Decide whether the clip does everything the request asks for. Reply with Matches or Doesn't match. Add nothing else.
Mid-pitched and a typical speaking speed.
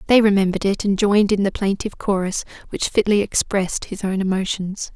Doesn't match